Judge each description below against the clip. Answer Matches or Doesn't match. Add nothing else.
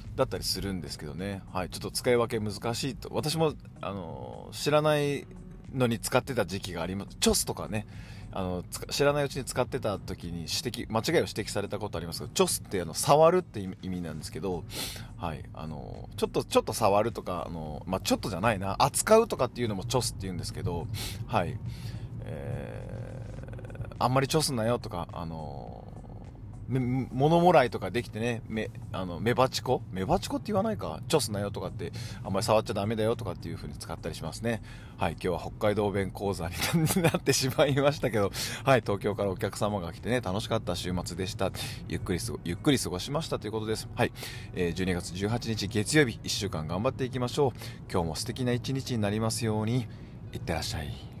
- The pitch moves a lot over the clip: Doesn't match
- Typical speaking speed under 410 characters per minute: Doesn't match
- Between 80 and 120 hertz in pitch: Matches